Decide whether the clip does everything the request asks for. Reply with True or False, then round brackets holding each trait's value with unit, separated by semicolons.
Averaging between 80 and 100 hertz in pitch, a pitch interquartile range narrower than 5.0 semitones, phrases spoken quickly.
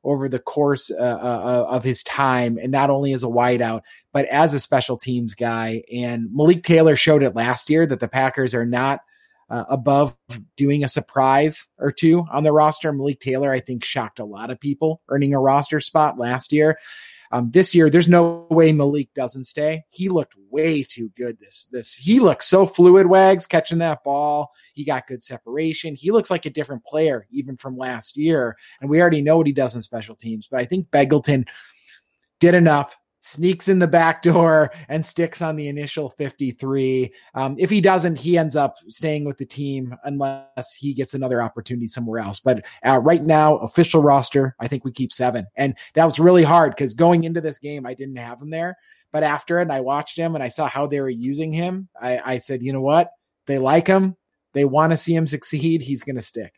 False (140 Hz; 4.0 semitones; 210 wpm)